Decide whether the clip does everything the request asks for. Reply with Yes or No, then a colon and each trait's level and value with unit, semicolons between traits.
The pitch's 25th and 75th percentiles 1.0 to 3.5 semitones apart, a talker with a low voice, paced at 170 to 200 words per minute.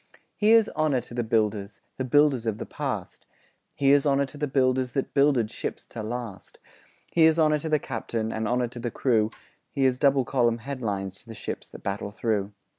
No: average, 4.0 semitones; low, 125 Hz; average, 190 wpm